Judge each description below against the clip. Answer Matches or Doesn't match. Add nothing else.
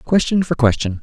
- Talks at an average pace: Matches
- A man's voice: Matches